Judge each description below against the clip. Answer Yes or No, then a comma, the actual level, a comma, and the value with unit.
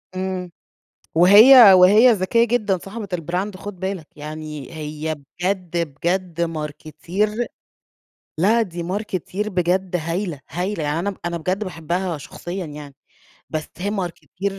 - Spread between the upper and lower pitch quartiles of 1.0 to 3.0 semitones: No, average, 3.4 semitones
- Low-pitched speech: No, medium, 180 Hz